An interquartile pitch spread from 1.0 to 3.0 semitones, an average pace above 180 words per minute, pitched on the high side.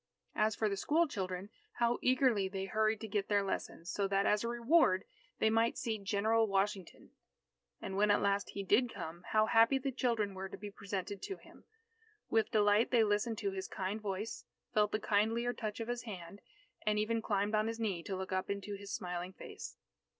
Yes: narrow, 2.4 semitones; average, 200 wpm; high, 210 Hz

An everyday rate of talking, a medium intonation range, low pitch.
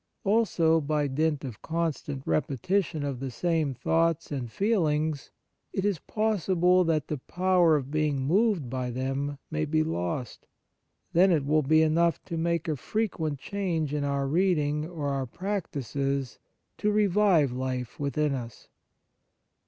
No: average, 145 wpm; average, 4.0 semitones; medium, 155 Hz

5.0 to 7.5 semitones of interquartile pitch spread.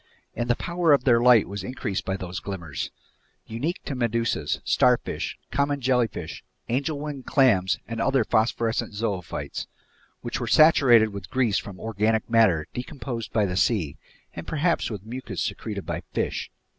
No: average, 4.6 semitones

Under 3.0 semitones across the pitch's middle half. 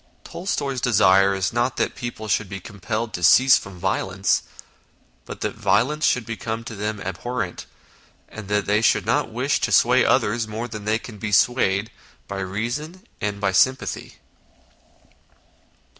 No: average, 3.5 semitones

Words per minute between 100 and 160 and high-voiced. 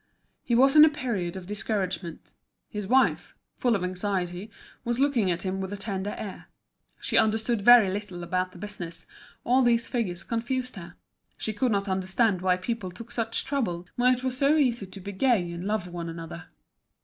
No: average, 185 wpm; high, 205 Hz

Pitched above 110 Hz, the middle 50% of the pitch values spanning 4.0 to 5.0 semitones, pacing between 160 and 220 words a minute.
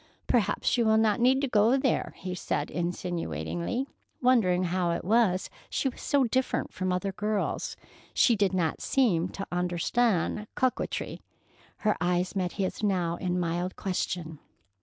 No: high, 190 Hz; average, 4.3 semitones; average, 150 wpm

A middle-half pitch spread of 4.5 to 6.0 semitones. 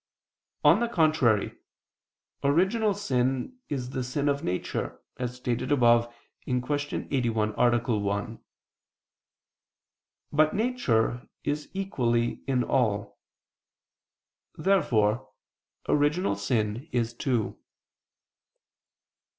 No: average, 4.1 semitones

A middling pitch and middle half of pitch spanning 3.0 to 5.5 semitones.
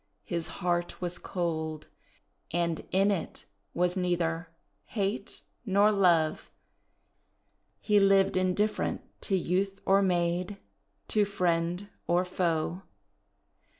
No: medium, 180 Hz; narrow, 2.4 semitones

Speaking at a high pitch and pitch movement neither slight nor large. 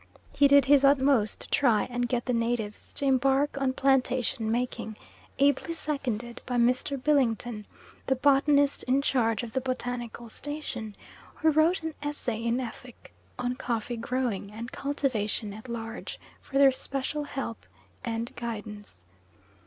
Yes: very high, 250 Hz; average, 3.2 semitones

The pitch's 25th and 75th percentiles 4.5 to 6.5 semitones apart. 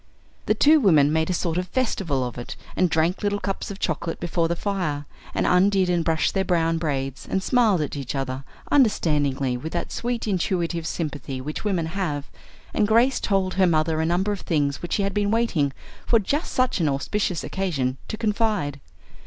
Yes: average, 5.2 semitones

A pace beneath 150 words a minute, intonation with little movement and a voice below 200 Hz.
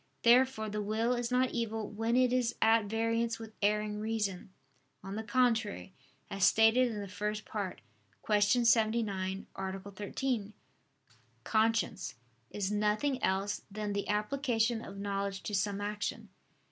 No: average, 140 wpm; narrow, 2.1 semitones; high, 215 Hz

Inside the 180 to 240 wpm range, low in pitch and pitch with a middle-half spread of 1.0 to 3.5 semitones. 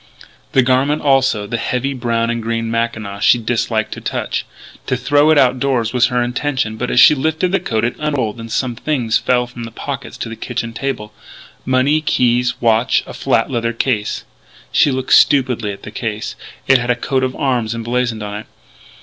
Yes: average, 200 wpm; low, 120 Hz; narrow, 2.5 semitones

